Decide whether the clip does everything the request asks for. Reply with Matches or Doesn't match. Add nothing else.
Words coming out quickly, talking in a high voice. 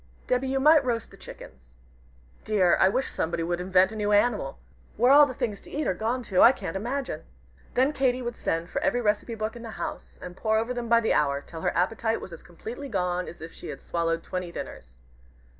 Matches